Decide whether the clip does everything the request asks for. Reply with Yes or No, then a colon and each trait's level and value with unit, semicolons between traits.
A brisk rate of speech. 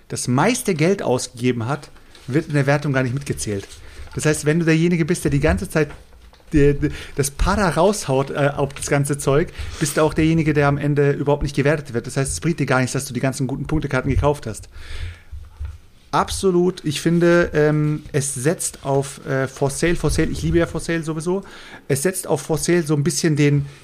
Yes: fast, 215 wpm